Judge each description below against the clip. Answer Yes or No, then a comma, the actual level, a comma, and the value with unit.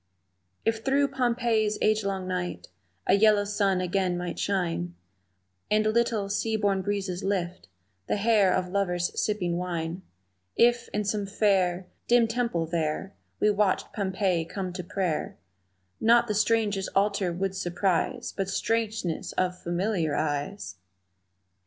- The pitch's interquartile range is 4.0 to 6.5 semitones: No, average, 3.2 semitones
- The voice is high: Yes, high, 195 Hz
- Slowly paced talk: Yes, slow, 130 wpm